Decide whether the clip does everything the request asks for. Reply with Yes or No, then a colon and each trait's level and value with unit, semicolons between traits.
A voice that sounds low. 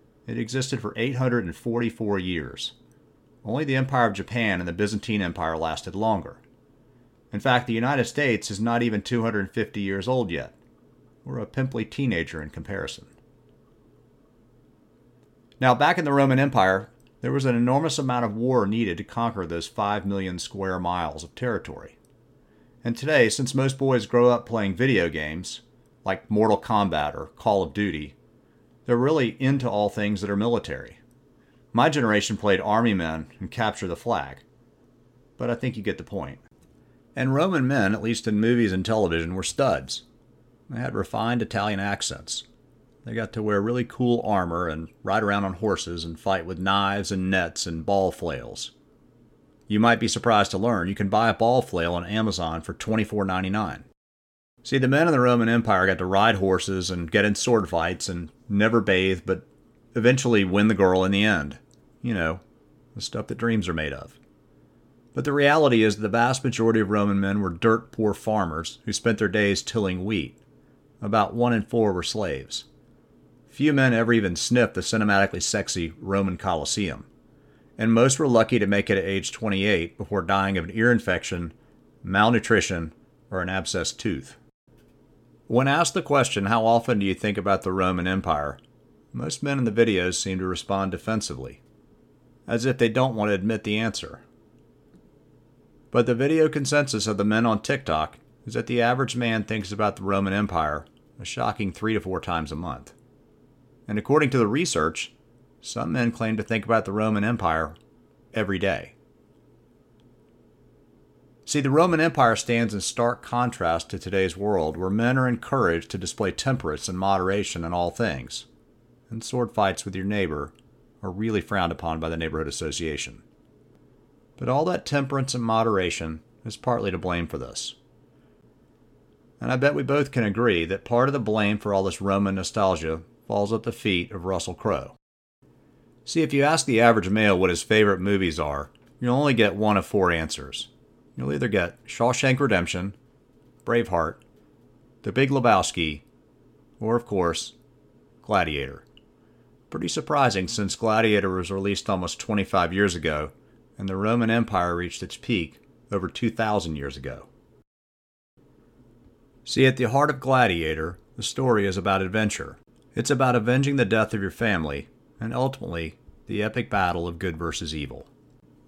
Yes: low, 105 Hz